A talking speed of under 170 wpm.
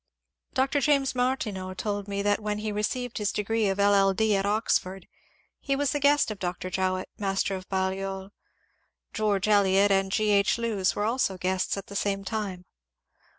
No: average, 180 wpm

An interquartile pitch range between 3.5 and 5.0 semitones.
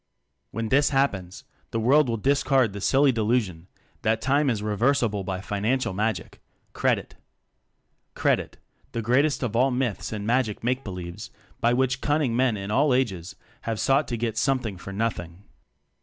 Yes: average, 4.3 semitones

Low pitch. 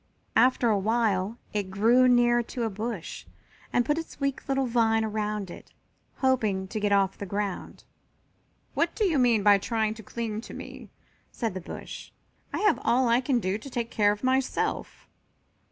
No: high, 225 Hz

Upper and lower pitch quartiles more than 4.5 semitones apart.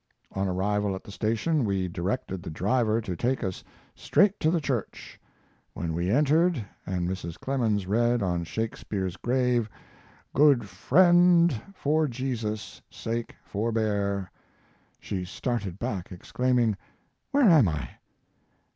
Yes: wide, 5.4 semitones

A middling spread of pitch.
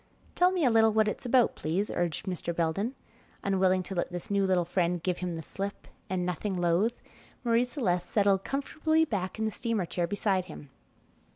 Yes: average, 4.2 semitones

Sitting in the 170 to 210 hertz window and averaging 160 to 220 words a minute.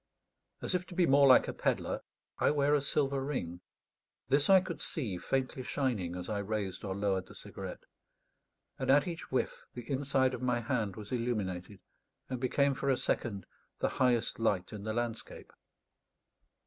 No: low, 125 Hz; average, 175 wpm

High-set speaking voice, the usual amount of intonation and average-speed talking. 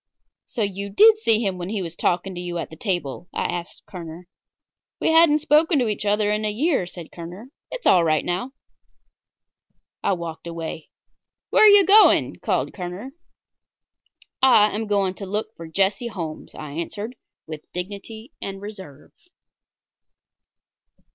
Yes: high, 195 Hz; average, 4.4 semitones; average, 155 wpm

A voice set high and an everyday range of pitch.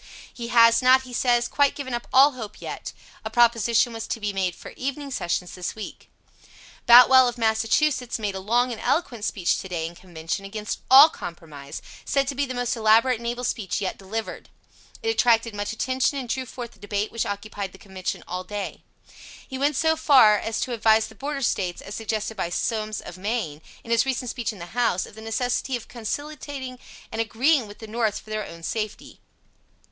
Yes: high, 225 Hz; average, 3.6 semitones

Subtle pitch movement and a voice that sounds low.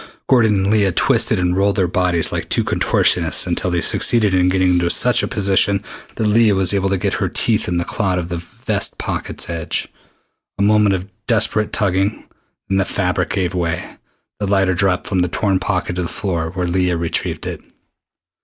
Yes: narrow, 2.3 semitones; very low, 95 Hz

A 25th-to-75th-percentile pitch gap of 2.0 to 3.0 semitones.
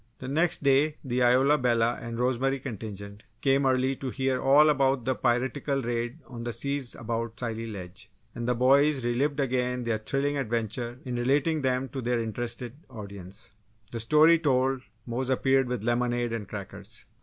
Yes: narrow, 2.5 semitones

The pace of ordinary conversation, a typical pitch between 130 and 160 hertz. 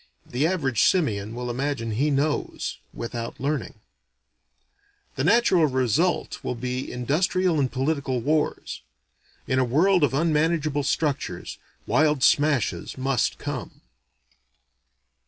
No: slow, 110 wpm; medium, 140 Hz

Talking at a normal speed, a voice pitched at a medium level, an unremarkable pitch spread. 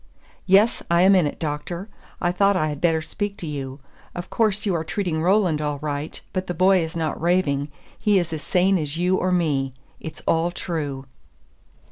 Yes: average, 195 wpm; medium, 170 Hz; average, 3.5 semitones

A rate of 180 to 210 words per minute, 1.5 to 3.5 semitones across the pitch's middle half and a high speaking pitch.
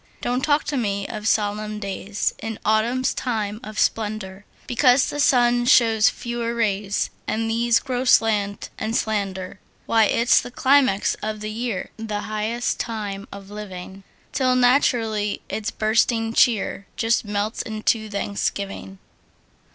No: slow, 135 wpm; narrow, 2.5 semitones; high, 220 Hz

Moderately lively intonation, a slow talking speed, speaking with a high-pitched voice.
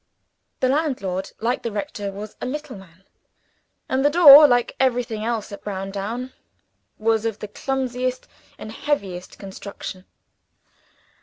Yes: average, 4.5 semitones; slow, 130 wpm; high, 225 Hz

